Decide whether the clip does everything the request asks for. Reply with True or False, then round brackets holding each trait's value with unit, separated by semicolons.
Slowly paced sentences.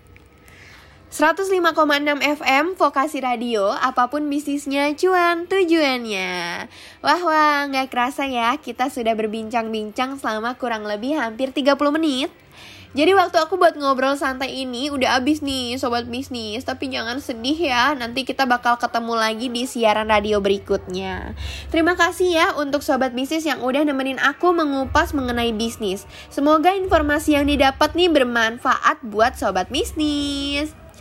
False (135 wpm)